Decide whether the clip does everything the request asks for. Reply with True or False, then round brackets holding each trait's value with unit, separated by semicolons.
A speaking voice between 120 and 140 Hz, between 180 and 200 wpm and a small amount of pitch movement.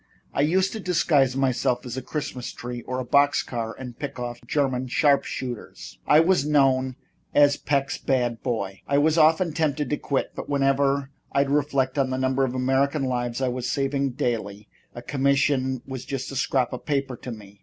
True (135 Hz; 190 wpm; 2.2 semitones)